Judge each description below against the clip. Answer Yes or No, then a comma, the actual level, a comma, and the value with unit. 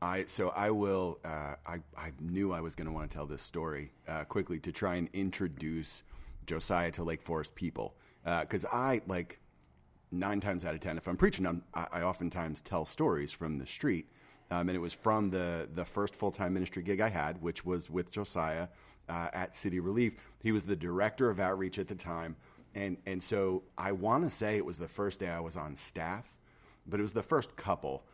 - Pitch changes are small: No, average, 3.1 semitones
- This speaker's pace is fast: Yes, fast, 215 wpm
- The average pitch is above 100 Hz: No, very low, 90 Hz